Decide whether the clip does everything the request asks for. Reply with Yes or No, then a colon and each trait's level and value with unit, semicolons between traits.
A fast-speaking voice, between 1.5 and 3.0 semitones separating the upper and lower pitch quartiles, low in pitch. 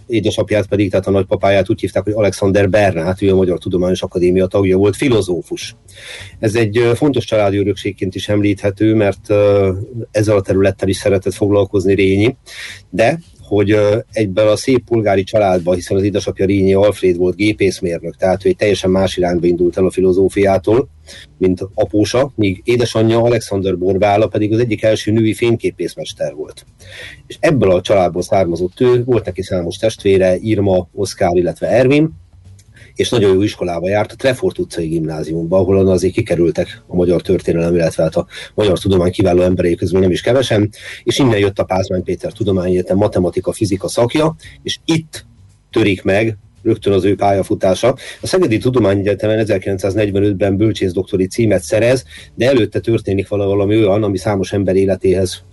Yes: fast, 160 wpm; narrow, 2.6 semitones; low, 100 Hz